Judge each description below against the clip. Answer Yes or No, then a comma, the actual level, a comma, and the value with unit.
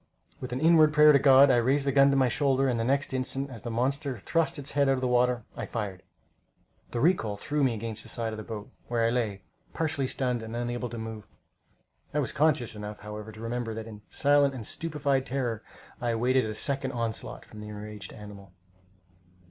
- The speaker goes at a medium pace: No, fast, 210 wpm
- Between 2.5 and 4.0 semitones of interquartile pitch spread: Yes, average, 3.7 semitones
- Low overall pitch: Yes, low, 125 Hz